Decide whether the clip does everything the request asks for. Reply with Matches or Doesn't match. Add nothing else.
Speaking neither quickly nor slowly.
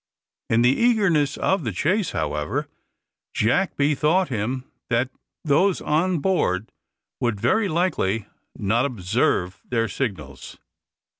Doesn't match